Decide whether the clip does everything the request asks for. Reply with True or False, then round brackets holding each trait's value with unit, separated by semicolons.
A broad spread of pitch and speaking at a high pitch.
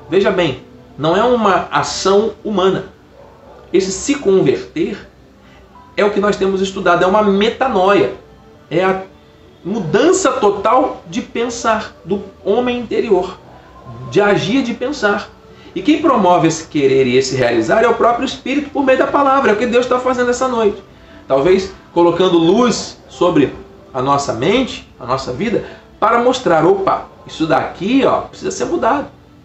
True (6.4 semitones; 200 Hz)